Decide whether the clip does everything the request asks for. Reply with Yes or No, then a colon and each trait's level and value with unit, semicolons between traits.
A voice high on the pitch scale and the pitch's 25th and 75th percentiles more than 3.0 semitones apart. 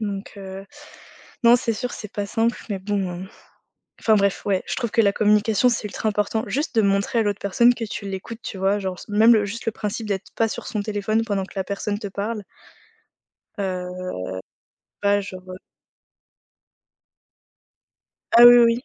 No: high, 205 Hz; narrow, 2.4 semitones